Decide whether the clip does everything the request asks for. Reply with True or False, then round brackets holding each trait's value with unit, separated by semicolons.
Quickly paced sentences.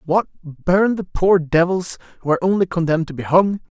False (190 wpm)